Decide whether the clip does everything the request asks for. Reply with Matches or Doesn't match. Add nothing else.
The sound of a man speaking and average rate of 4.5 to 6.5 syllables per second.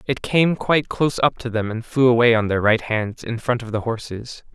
Matches